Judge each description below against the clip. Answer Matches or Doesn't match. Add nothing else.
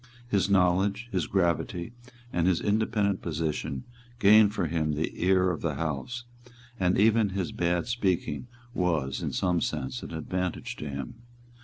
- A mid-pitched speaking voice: Doesn't match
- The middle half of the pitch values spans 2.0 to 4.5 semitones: Matches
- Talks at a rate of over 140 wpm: Matches